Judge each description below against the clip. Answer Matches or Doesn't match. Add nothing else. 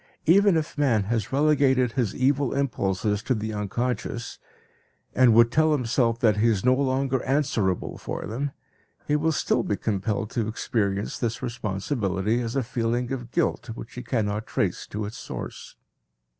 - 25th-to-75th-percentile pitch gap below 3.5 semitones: Doesn't match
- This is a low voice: Matches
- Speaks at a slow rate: Doesn't match